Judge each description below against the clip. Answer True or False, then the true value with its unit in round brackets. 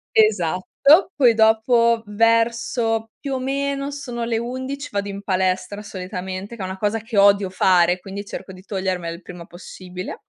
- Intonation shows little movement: False (3.9 semitones)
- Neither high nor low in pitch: False (210 Hz)